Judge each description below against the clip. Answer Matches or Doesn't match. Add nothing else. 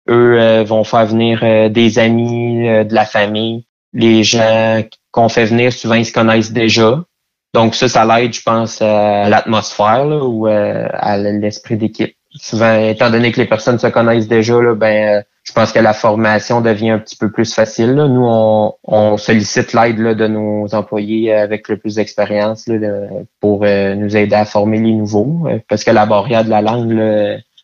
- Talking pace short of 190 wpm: Doesn't match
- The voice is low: Matches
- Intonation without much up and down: Matches